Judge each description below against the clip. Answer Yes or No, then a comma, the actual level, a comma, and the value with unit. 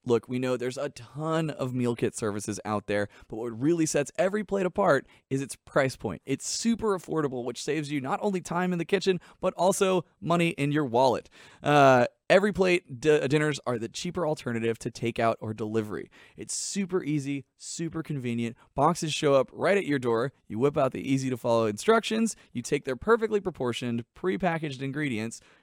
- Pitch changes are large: Yes, wide, 6.5 semitones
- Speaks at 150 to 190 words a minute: Yes, average, 185 wpm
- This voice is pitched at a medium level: Yes, medium, 145 Hz